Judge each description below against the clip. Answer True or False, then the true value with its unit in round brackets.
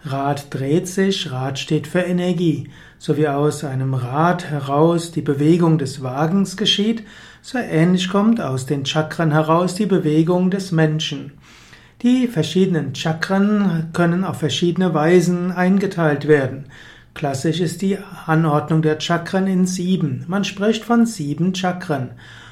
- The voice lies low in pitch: False (165 Hz)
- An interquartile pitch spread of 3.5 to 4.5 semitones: True (3.8 semitones)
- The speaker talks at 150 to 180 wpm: False (135 wpm)